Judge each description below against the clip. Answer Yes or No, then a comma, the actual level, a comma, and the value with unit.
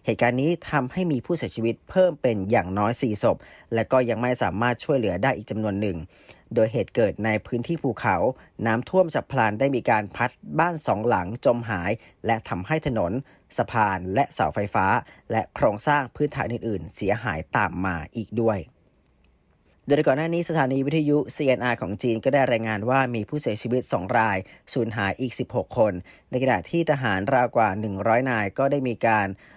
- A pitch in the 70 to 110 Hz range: No, low, 120 Hz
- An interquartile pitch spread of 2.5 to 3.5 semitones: No, average, 4.3 semitones